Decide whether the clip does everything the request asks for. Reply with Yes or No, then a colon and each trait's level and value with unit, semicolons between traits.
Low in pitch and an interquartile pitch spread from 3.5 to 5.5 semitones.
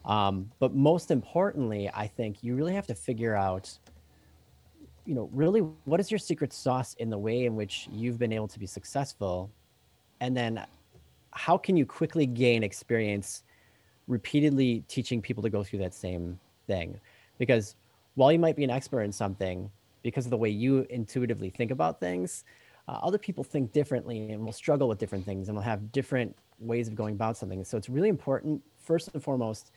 Yes: low, 115 Hz; average, 4.6 semitones